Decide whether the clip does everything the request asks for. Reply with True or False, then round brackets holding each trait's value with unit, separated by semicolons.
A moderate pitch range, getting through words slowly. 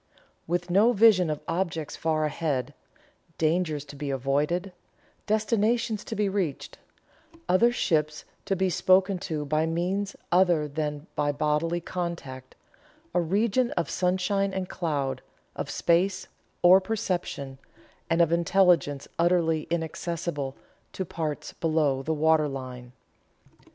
True (3.8 semitones; 120 wpm)